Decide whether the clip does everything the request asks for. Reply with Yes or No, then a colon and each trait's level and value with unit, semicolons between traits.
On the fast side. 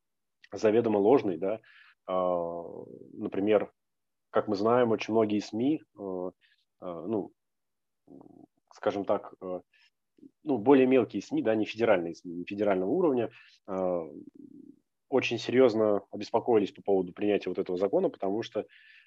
No: slow, 110 wpm